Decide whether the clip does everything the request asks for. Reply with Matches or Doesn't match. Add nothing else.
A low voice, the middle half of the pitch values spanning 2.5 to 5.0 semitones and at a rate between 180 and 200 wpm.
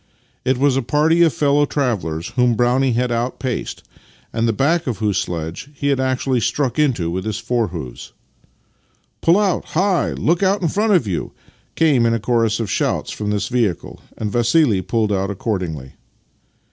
Doesn't match